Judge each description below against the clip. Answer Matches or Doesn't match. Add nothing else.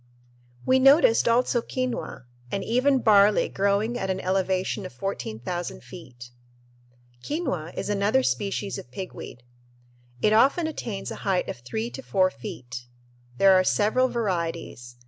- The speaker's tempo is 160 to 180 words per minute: Doesn't match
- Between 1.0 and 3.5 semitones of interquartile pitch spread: Doesn't match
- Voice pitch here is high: Matches